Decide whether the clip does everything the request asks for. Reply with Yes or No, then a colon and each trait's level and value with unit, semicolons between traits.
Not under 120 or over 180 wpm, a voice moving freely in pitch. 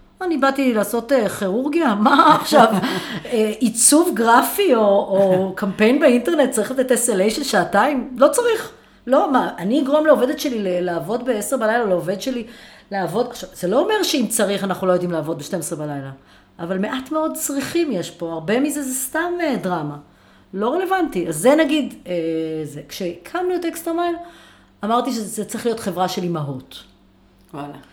Yes: fast, 150 wpm; wide, 7.8 semitones